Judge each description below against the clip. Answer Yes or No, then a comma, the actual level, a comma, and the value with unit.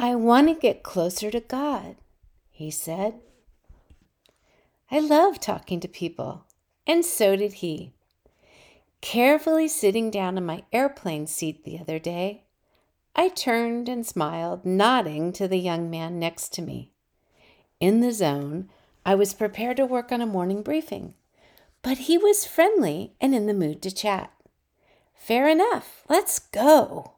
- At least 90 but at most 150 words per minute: Yes, average, 145 wpm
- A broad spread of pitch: Yes, wide, 7.5 semitones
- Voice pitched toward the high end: Yes, high, 205 Hz